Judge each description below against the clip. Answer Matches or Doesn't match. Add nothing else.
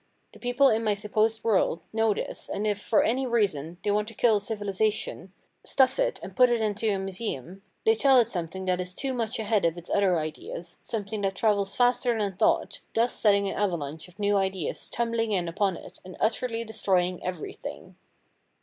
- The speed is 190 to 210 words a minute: Matches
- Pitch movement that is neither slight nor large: Matches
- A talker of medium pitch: Doesn't match